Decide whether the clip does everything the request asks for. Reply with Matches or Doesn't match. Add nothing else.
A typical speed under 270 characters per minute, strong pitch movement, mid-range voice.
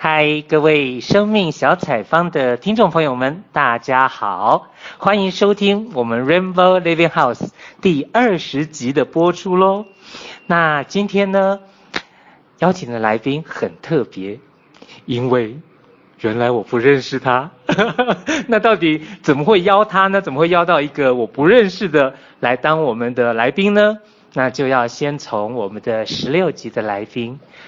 Matches